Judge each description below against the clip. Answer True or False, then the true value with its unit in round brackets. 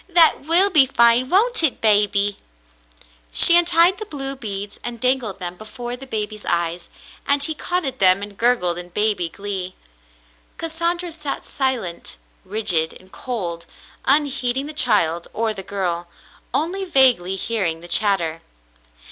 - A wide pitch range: True (7.3 semitones)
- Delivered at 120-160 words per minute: True (150 wpm)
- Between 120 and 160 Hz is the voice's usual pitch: False (225 Hz)